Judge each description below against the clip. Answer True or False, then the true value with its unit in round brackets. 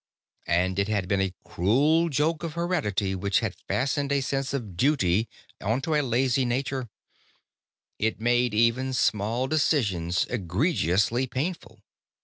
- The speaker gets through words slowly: True (130 wpm)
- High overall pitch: False (120 Hz)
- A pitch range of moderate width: False (5.7 semitones)